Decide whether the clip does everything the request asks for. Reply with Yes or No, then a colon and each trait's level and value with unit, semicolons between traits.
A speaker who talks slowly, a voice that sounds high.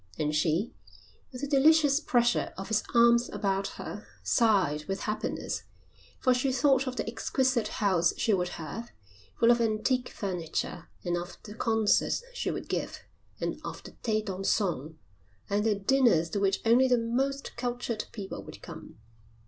No: average, 160 wpm; high, 220 Hz